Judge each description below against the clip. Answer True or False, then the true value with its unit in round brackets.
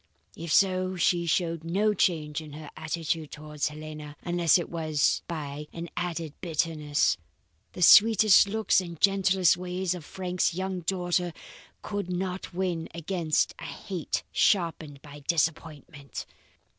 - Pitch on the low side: False (170 Hz)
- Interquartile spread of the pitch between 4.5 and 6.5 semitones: False (3.1 semitones)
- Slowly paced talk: True (130 wpm)